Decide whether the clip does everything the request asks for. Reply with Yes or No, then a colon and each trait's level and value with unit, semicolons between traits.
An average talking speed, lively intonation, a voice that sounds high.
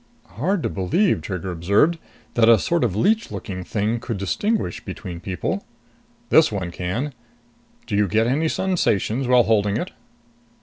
No: average, 155 wpm; wide, 7.6 semitones; low, 110 Hz